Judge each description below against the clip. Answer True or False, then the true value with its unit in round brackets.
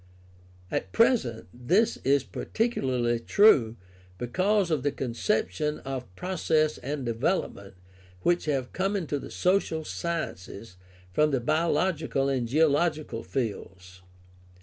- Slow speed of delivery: True (110 wpm)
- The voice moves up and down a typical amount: False (6.0 semitones)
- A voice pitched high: False (145 Hz)